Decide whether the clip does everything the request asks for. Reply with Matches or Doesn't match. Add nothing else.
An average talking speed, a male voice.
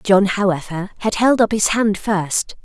Doesn't match